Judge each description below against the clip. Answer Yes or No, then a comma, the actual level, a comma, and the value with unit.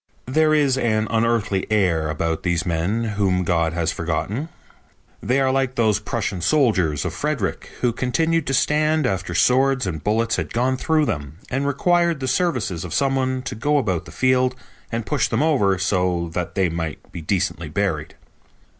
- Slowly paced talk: No, average, 175 wpm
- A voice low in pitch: Yes, low, 115 Hz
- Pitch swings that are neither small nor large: No, wide, 7.0 semitones